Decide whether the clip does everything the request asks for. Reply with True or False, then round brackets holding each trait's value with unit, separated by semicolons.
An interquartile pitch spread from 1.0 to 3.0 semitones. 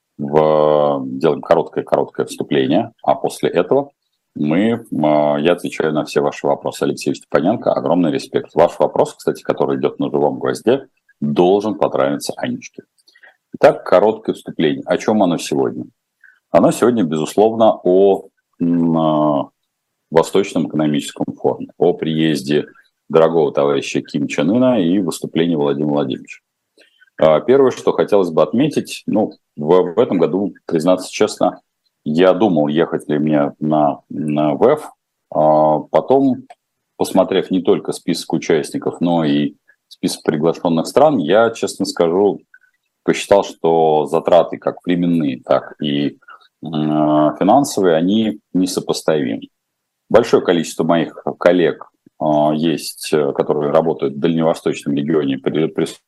True (2.7 semitones)